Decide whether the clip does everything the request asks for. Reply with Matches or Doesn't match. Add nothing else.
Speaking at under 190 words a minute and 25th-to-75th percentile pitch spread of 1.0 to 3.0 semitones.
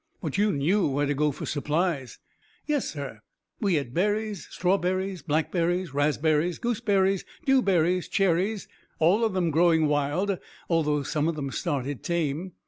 Doesn't match